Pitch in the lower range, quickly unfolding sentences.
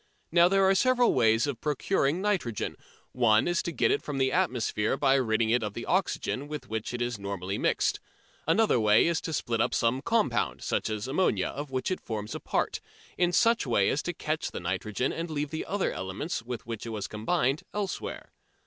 Yes: low, 130 Hz; fast, 210 wpm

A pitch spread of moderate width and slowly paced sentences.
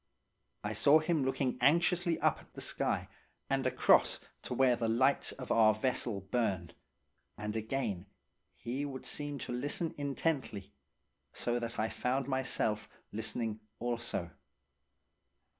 Yes: average, 4.1 semitones; slow, 130 wpm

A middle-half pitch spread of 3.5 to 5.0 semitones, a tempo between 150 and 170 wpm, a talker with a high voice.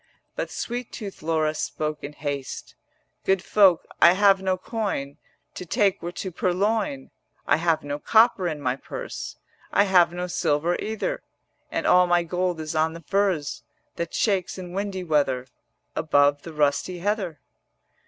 No: average, 4.0 semitones; average, 160 wpm; medium, 175 Hz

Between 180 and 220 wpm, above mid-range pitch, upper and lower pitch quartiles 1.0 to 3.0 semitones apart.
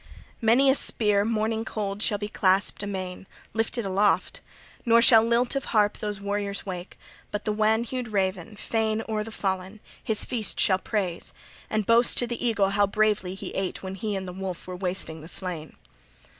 Yes: average, 185 wpm; high, 205 Hz; average, 2.7 semitones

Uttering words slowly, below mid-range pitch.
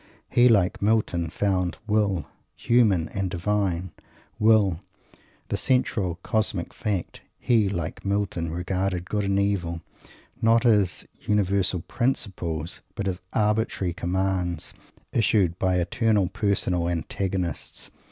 Yes: slow, 110 wpm; very low, 95 Hz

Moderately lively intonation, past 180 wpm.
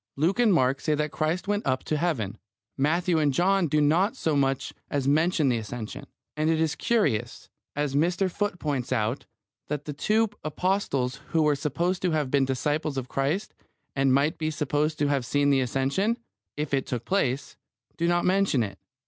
Yes: average, 4.3 semitones; average, 190 wpm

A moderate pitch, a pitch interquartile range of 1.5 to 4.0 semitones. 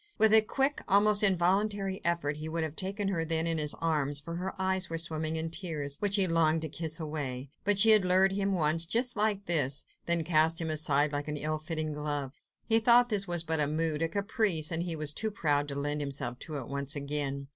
No: medium, 165 Hz; average, 4.4 semitones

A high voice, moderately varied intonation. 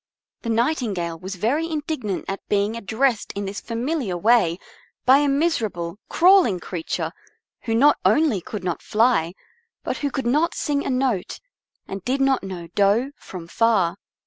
No: high, 230 Hz; wide, 6.1 semitones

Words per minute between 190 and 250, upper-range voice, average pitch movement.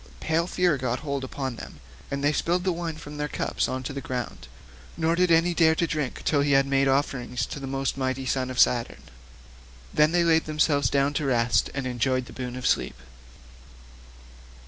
No: average, 195 wpm; medium, 140 Hz; average, 3.6 semitones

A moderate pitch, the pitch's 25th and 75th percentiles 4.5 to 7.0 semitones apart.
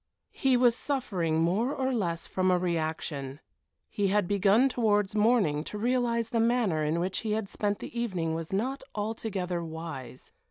No: high, 200 Hz; wide, 5.6 semitones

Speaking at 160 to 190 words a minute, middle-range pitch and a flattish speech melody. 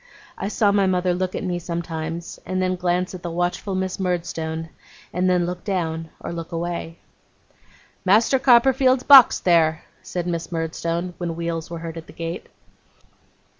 Yes: average, 165 wpm; medium, 175 Hz; narrow, 1.9 semitones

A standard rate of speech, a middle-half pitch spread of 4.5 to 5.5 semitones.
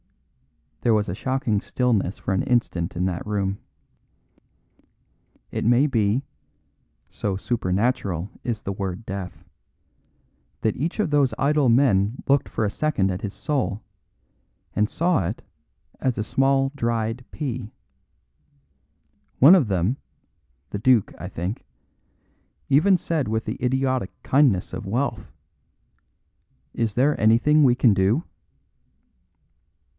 No: slow, 125 wpm; average, 5.2 semitones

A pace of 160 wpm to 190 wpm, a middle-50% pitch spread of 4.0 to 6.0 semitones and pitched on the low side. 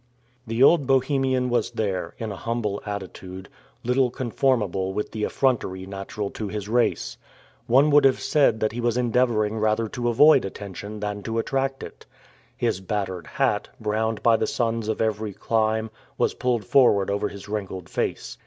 No: average, 165 wpm; average, 3.3 semitones; low, 110 Hz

